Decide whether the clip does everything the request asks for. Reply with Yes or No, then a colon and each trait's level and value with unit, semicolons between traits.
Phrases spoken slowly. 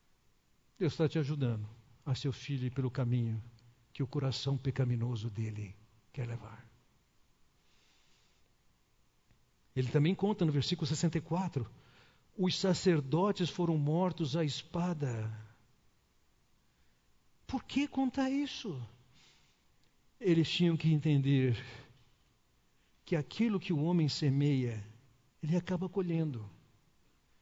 Yes: slow, 100 wpm